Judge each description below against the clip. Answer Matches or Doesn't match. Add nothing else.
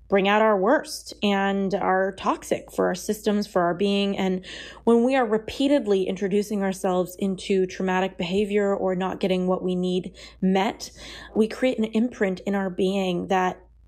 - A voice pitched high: Matches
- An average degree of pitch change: Doesn't match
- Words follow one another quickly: Doesn't match